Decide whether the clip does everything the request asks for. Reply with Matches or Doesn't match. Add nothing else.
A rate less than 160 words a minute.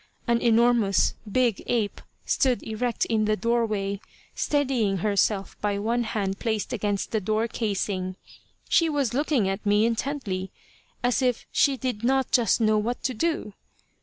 Matches